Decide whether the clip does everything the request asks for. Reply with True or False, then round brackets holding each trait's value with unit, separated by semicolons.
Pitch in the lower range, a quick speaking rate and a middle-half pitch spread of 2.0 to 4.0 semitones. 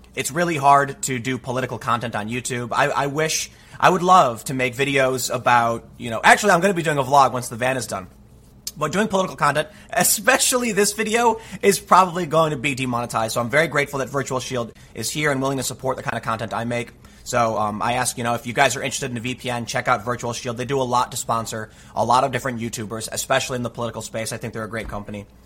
True (130 Hz; 250 wpm; 3.3 semitones)